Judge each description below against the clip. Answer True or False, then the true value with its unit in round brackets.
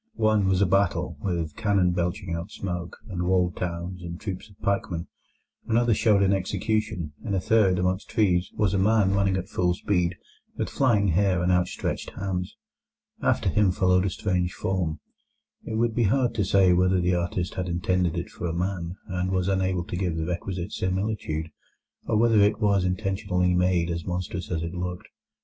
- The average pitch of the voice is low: True (90 Hz)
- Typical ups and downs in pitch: False (2.1 semitones)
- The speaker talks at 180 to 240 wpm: True (185 wpm)